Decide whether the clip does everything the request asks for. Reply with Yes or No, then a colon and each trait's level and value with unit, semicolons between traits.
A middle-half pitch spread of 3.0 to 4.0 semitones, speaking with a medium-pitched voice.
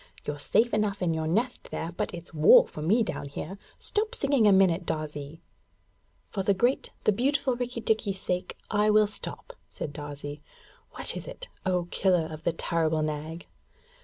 No: wide, 5.5 semitones; medium, 180 Hz